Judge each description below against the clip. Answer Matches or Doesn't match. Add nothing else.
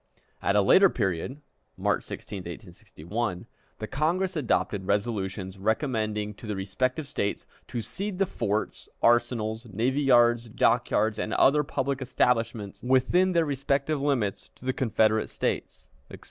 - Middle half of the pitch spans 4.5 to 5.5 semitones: Matches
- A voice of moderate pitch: Doesn't match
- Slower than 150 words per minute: Matches